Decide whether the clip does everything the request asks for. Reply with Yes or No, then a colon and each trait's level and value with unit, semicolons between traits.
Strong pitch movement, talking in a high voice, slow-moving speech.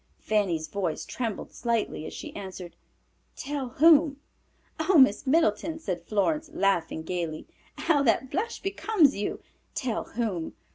Yes: wide, 8.2 semitones; high, 230 Hz; slow, 130 wpm